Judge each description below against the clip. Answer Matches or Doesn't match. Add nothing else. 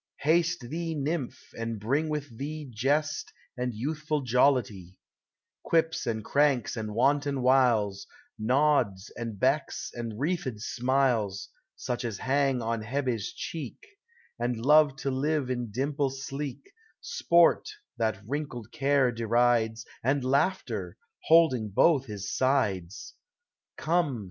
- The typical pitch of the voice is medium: Doesn't match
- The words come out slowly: Matches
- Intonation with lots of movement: Doesn't match